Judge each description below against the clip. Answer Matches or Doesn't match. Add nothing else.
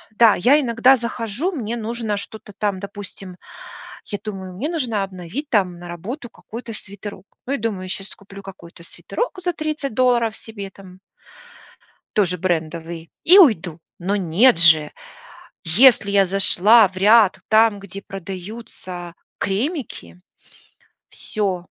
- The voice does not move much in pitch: Doesn't match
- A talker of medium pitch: Doesn't match